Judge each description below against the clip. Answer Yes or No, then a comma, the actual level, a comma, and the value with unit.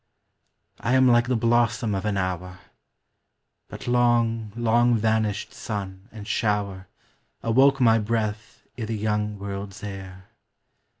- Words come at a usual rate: No, slow, 125 wpm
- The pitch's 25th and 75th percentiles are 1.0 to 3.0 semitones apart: Yes, average, 2.7 semitones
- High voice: No, low, 110 Hz